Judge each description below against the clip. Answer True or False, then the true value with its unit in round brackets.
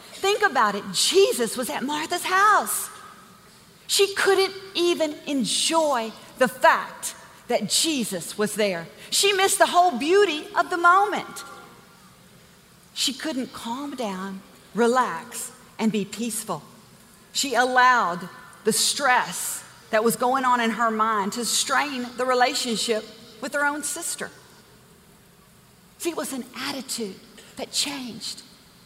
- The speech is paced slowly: True (125 wpm)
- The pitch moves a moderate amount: False (6.4 semitones)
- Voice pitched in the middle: False (250 Hz)